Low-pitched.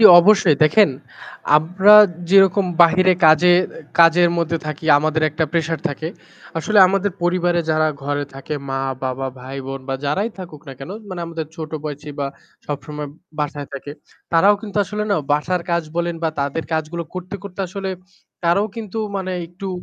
No: medium, 170 Hz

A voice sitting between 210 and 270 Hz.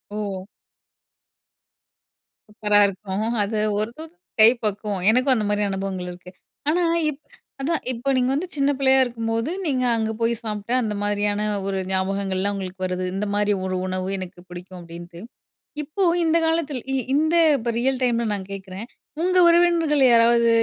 Yes: high, 215 Hz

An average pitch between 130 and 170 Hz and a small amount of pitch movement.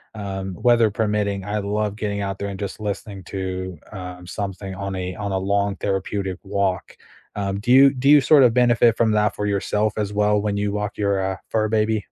No: low, 100 Hz; narrow, 1.7 semitones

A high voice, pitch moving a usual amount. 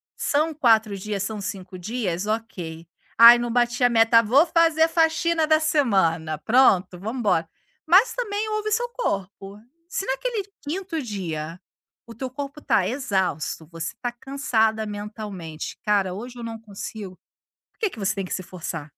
No: high, 225 Hz; wide, 7.1 semitones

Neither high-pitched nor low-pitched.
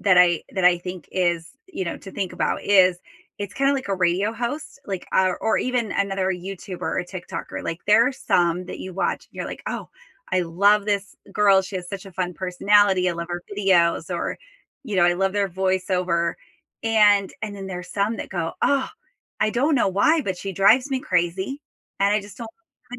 No: high, 195 Hz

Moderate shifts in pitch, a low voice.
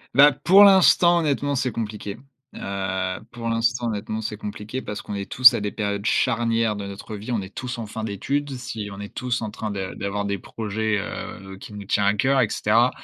Yes: average, 3.4 semitones; low, 110 Hz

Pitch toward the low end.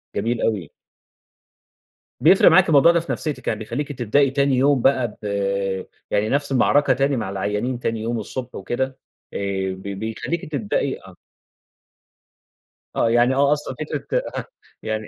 Yes: low, 125 Hz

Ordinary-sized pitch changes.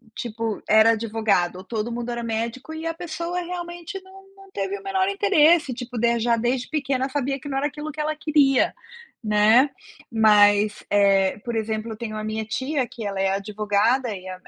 No: wide, 6.1 semitones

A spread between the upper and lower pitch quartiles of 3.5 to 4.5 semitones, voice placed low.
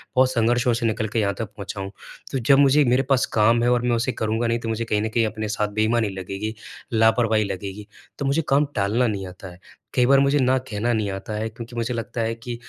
No: narrow, 2.4 semitones; low, 115 Hz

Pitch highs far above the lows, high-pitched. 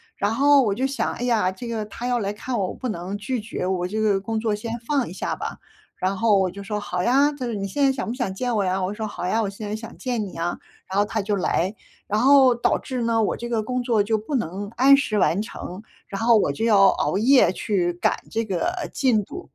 No: average, 3.6 semitones; high, 215 Hz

